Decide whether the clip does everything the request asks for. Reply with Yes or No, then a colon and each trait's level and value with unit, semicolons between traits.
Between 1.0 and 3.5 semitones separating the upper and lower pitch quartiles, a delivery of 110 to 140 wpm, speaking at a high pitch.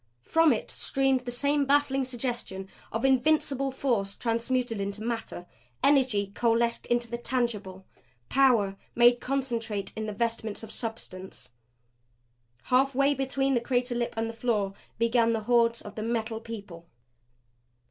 Yes: average, 2.9 semitones; slow, 135 wpm; high, 235 Hz